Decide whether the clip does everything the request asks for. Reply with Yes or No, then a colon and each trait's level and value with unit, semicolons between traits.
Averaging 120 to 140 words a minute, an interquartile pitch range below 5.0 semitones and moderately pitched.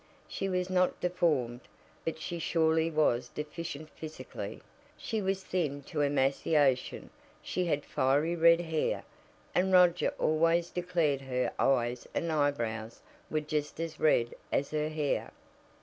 Yes: slow, 135 wpm; average, 3.3 semitones; medium, 155 Hz